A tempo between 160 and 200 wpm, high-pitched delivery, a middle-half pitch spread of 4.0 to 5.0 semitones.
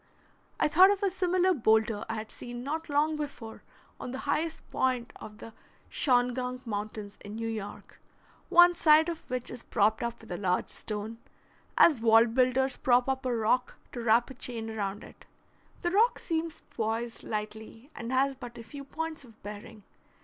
Yes: average, 180 wpm; high, 245 Hz; average, 4.7 semitones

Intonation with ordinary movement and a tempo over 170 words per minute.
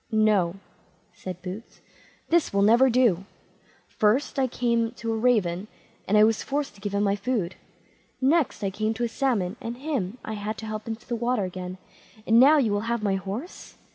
Yes: average, 3.7 semitones; average, 195 wpm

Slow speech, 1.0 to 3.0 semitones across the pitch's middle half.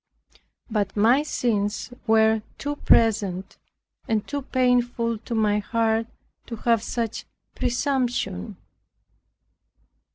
Yes: slow, 95 wpm; narrow, 2.5 semitones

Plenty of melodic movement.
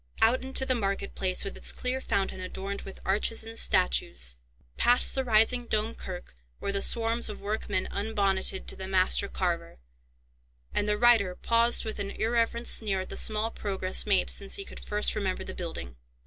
No: average, 3.2 semitones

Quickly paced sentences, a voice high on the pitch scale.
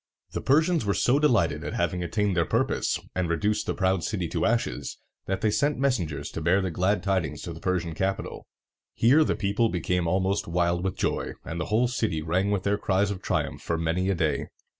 No: fast, 210 wpm; very low, 95 Hz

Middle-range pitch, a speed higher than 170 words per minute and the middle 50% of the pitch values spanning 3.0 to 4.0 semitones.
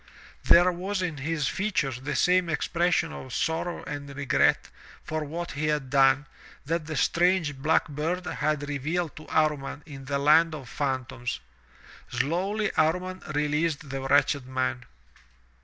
No: medium, 150 Hz; average, 145 wpm; average, 3.5 semitones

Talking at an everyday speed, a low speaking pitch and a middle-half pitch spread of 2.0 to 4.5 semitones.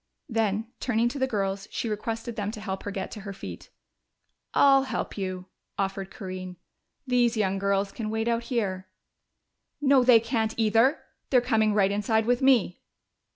No: average, 165 wpm; high, 220 Hz; average, 3.4 semitones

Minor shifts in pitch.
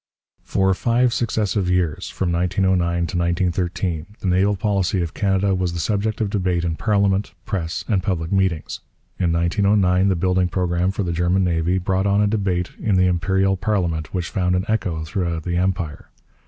Yes: narrow, 2.2 semitones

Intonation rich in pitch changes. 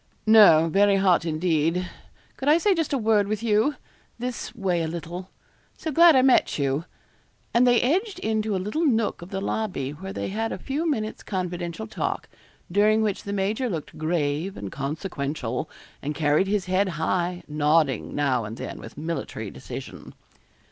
Yes: wide, 5.9 semitones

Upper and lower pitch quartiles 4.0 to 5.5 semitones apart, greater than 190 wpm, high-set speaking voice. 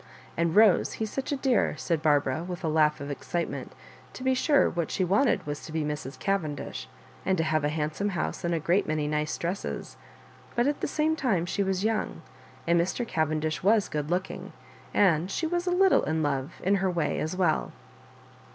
No: average, 5.0 semitones; average, 200 wpm; medium, 170 Hz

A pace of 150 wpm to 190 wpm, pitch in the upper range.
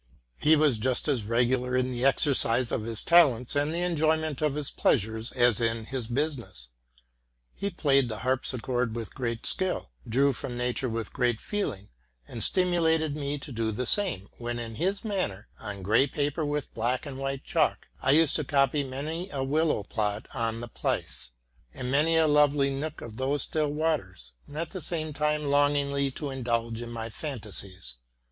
No: average, 175 wpm; low, 135 Hz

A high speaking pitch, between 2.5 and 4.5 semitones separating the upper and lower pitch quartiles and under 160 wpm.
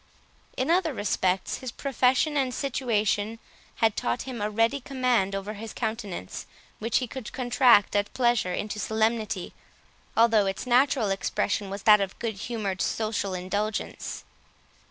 Yes: high, 220 Hz; average, 3.5 semitones; average, 140 wpm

